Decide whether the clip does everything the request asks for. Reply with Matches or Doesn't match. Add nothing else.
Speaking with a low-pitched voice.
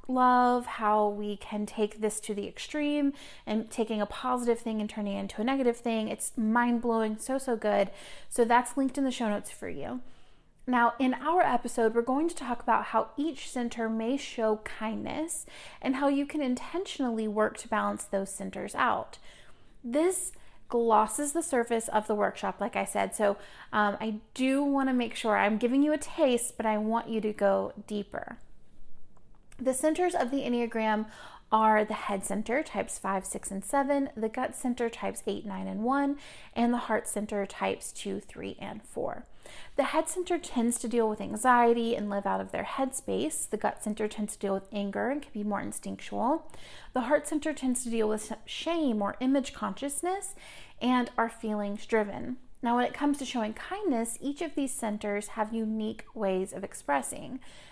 Doesn't match